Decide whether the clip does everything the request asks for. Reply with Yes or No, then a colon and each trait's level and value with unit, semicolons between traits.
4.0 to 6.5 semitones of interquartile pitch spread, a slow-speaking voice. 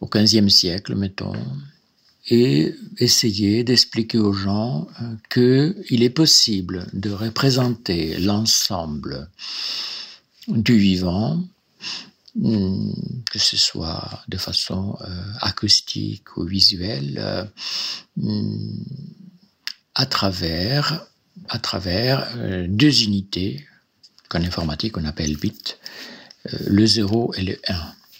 Yes: average, 4.6 semitones; slow, 85 wpm